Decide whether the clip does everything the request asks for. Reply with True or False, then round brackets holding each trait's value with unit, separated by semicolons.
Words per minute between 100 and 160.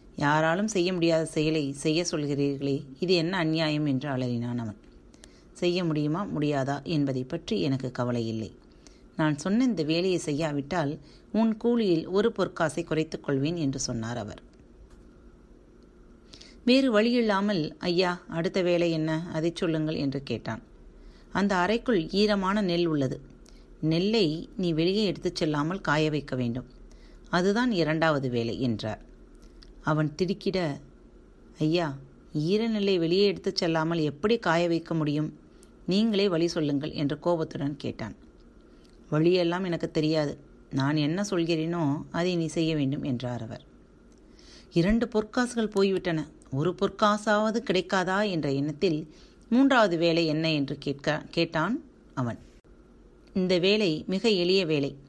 True (120 wpm)